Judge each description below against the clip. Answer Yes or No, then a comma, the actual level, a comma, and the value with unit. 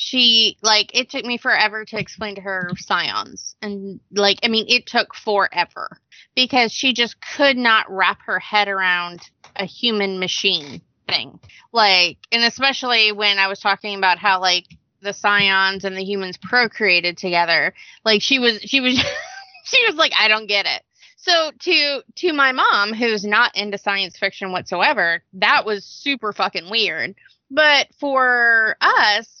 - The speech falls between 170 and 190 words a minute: No, average, 160 wpm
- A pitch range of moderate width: Yes, average, 4.2 semitones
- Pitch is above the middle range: Yes, high, 210 Hz